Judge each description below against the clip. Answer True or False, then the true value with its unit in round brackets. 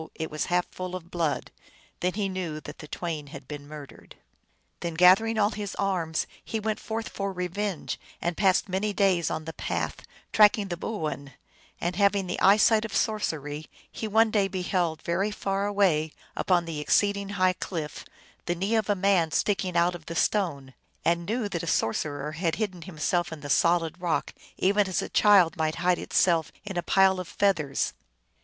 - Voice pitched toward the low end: False (180 Hz)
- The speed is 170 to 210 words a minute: True (185 wpm)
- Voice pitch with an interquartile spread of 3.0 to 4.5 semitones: True (3.7 semitones)